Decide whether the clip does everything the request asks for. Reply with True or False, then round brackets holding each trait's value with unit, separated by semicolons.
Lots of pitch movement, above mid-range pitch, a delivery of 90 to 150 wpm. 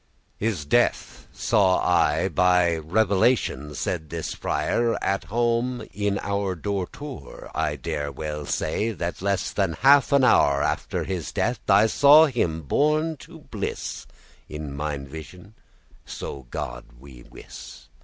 False (6.9 semitones; 95 Hz; 140 wpm)